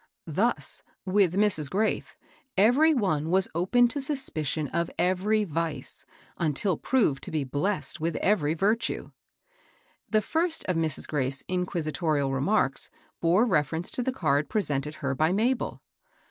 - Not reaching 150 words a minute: Yes, slow, 135 wpm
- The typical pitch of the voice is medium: Yes, medium, 180 Hz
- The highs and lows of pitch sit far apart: Yes, wide, 5.8 semitones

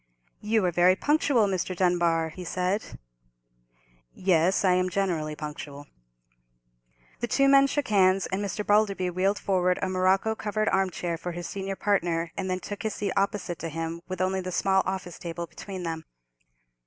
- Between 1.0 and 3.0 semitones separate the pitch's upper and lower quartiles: Yes, narrow, 2.4 semitones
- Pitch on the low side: No, medium, 185 Hz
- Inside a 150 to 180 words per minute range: Yes, average, 170 wpm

